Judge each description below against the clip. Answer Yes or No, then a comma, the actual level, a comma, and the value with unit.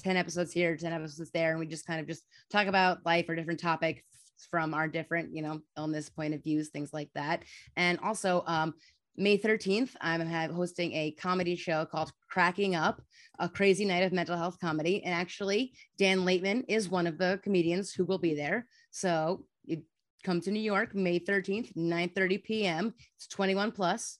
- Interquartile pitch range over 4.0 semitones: No, average, 3.0 semitones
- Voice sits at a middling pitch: Yes, medium, 175 Hz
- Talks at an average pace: Yes, average, 190 wpm